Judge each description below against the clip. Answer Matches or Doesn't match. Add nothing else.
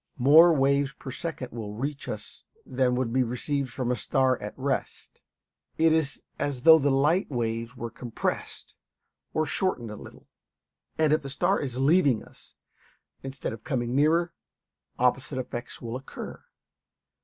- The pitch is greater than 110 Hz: Matches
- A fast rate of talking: Doesn't match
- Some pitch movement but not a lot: Matches